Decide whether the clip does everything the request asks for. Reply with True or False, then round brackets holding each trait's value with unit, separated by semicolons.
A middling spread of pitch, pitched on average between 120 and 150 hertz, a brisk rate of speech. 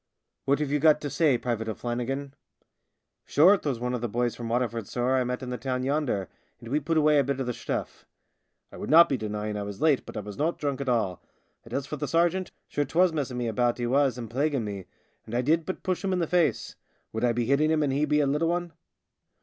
True (4.1 semitones; 135 Hz; 265 wpm)